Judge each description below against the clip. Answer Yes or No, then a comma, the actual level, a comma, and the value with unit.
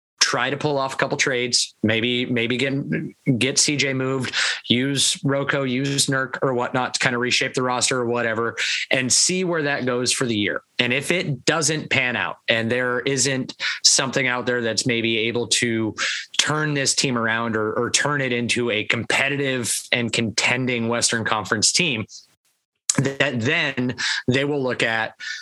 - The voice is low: Yes, low, 125 Hz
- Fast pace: No, average, 175 wpm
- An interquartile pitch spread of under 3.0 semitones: Yes, narrow, 2.4 semitones